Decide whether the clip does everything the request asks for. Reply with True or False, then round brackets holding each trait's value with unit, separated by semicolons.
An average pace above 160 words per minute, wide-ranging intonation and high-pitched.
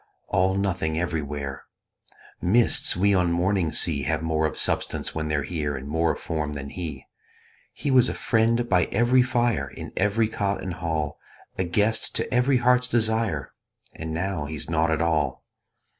False (170 wpm; 6.0 semitones; 85 Hz)